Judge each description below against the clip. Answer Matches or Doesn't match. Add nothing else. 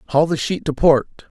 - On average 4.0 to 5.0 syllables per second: Matches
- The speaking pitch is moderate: Matches